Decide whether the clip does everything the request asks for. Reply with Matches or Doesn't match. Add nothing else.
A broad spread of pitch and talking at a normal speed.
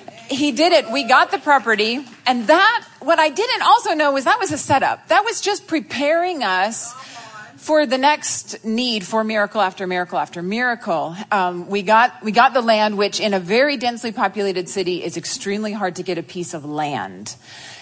Matches